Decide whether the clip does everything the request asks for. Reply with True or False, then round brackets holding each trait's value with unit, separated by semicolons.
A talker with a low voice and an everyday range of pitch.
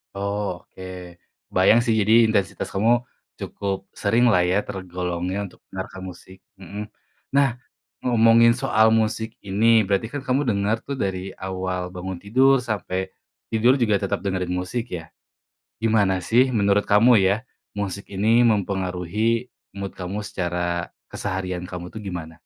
True (100 Hz; 3.3 semitones)